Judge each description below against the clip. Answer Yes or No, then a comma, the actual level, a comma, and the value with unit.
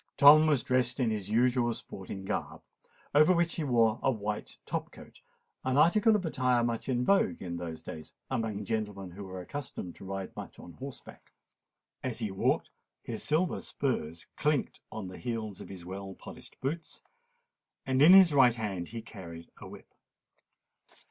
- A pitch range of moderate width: No, wide, 6.1 semitones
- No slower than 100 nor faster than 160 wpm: No, average, 170 wpm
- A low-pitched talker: Yes, low, 115 Hz